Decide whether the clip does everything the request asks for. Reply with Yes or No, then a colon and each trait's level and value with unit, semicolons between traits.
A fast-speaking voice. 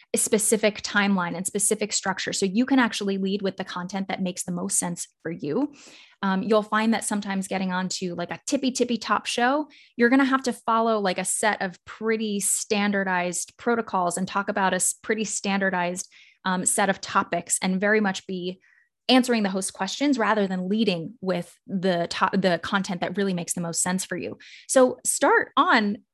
No: average, 190 wpm